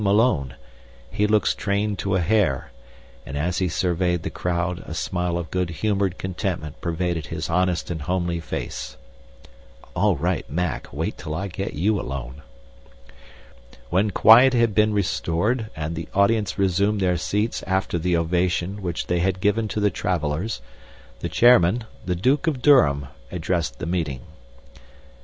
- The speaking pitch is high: No, very low, 90 Hz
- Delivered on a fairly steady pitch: No, average, 3.6 semitones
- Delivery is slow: No, average, 150 wpm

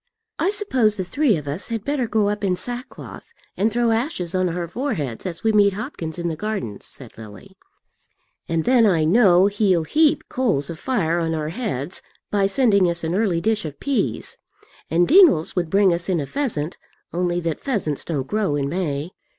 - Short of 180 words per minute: No, average, 190 wpm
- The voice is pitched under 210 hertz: Yes, medium, 185 Hz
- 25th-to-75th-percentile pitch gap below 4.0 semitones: No, wide, 5.5 semitones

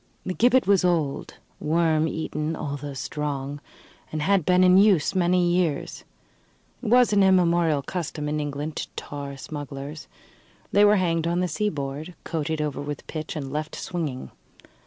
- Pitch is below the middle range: No, medium, 160 Hz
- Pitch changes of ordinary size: Yes, average, 3.7 semitones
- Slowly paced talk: No, average, 155 wpm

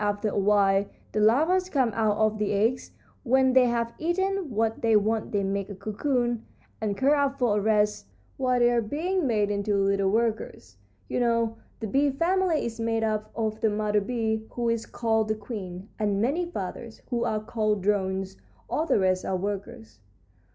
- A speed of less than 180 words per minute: No, average, 185 wpm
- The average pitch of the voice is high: Yes, high, 220 Hz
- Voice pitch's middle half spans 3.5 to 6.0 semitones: No, average, 3.1 semitones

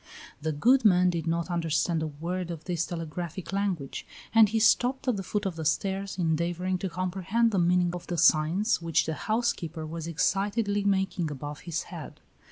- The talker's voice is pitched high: No, medium, 175 Hz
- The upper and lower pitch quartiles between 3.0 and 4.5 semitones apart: Yes, average, 3.3 semitones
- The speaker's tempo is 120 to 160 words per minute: No, average, 180 wpm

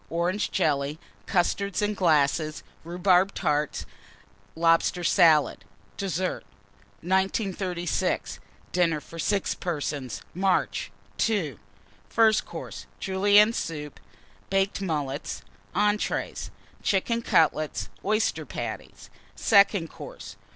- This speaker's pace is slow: Yes, slow, 90 wpm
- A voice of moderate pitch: Yes, medium, 180 Hz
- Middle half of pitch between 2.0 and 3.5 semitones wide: No, average, 4.0 semitones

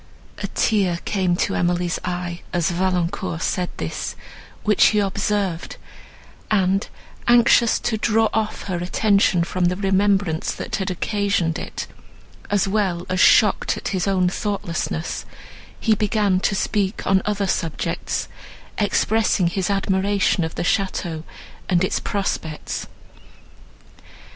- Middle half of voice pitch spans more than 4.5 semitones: No, narrow, 2.5 semitones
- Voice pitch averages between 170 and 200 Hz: Yes, high, 190 Hz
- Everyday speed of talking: No, slow, 125 wpm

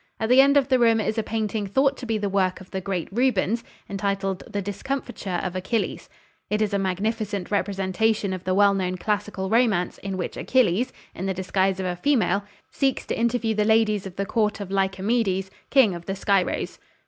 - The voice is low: No, high, 200 Hz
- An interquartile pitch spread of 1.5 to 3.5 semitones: Yes, average, 2.8 semitones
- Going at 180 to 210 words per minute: Yes, average, 200 wpm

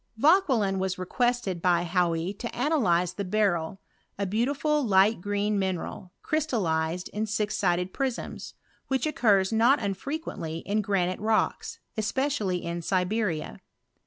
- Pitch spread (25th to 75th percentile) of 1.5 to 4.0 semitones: No, average, 4.8 semitones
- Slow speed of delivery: Yes, slow, 120 wpm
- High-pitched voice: Yes, high, 200 Hz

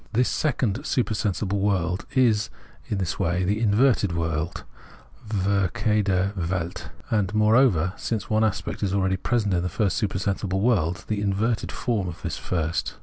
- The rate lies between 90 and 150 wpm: Yes, average, 145 wpm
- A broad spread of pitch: No, average, 3.0 semitones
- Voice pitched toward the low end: Yes, low, 100 Hz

